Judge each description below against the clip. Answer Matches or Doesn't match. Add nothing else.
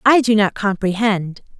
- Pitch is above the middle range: Matches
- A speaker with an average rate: Matches